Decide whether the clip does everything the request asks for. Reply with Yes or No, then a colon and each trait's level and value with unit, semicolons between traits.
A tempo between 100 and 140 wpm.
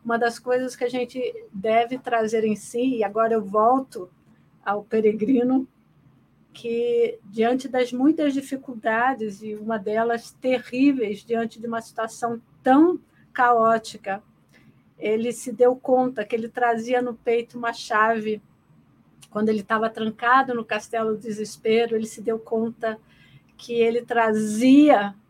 Yes: average, 135 wpm